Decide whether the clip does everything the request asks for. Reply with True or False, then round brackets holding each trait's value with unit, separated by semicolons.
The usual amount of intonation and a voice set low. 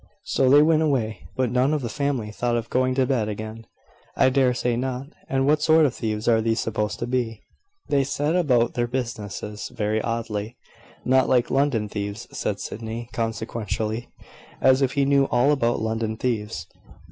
True (3.2 semitones; 120 Hz)